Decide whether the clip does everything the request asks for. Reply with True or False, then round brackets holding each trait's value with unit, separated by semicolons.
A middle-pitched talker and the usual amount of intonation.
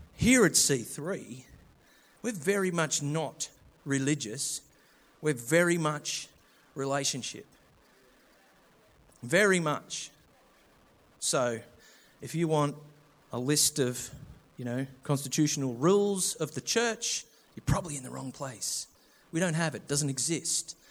True (150 Hz; 3.3 semitones)